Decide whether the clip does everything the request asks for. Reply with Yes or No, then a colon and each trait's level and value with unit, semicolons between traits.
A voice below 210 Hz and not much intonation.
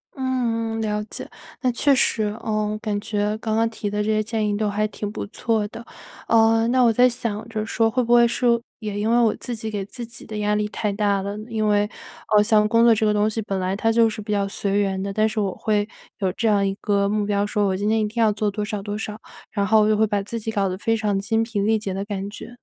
No: high, 215 Hz; narrow, 1.6 semitones